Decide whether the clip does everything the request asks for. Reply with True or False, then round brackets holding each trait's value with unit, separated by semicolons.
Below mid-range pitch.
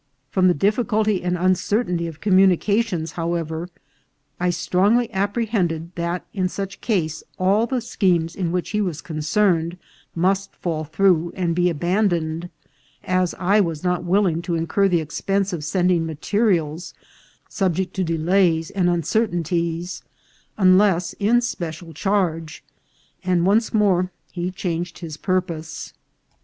False (180 Hz)